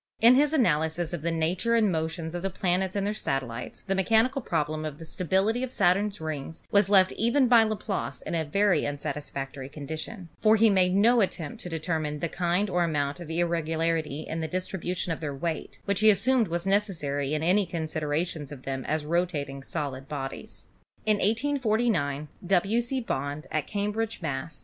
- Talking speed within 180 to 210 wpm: Yes, average, 185 wpm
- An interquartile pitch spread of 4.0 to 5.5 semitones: Yes, average, 5.2 semitones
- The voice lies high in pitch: No, medium, 170 Hz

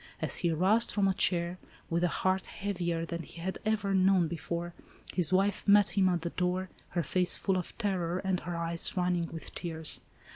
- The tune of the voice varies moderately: No, narrow, 2.0 semitones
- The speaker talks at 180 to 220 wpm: Yes, average, 195 wpm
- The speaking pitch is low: No, medium, 180 Hz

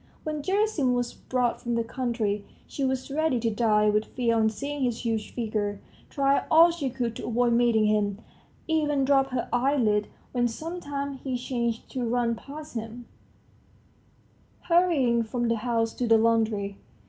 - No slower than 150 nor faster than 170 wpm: Yes, average, 160 wpm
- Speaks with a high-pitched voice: Yes, high, 240 Hz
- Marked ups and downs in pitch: No, average, 3.5 semitones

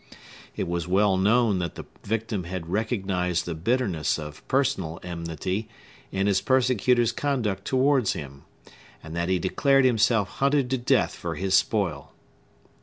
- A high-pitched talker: No, low, 100 Hz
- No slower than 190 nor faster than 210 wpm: No, average, 145 wpm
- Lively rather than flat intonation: Yes, wide, 5.8 semitones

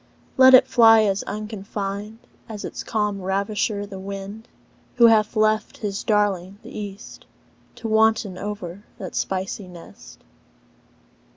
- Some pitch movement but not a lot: No, narrow, 1.9 semitones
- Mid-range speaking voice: No, high, 205 Hz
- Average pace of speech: No, slow, 125 wpm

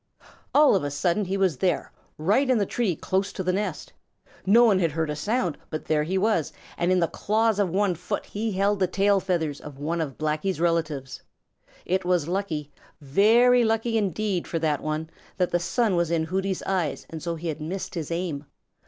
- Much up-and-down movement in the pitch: No, average, 4.0 semitones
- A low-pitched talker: No, medium, 180 Hz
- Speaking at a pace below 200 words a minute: No, fast, 205 wpm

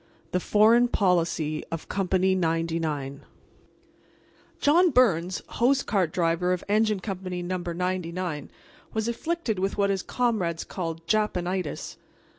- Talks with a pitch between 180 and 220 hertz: Yes, medium, 185 Hz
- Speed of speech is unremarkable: No, slow, 115 wpm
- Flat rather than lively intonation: No, average, 4.1 semitones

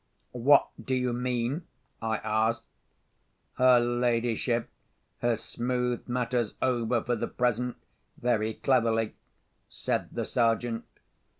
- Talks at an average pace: No, slow, 105 wpm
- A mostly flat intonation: Yes, narrow, 1.4 semitones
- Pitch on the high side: No, low, 120 Hz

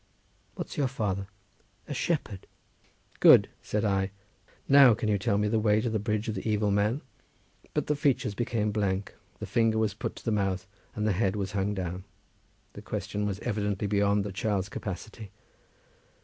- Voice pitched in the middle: No, low, 105 Hz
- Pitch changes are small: Yes, narrow, 1.9 semitones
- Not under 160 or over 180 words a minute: Yes, average, 175 wpm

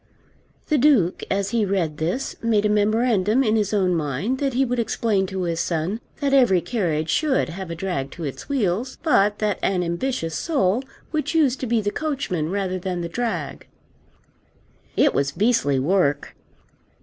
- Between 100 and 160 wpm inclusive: No, average, 175 wpm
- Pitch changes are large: Yes, wide, 6.1 semitones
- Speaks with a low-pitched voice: No, high, 200 Hz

